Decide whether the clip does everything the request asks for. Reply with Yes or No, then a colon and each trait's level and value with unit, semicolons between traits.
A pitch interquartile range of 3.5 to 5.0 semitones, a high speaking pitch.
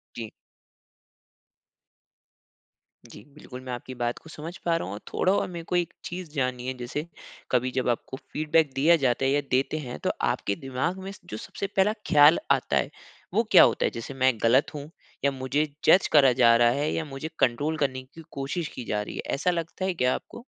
No: average, 4.5 semitones; medium, 140 Hz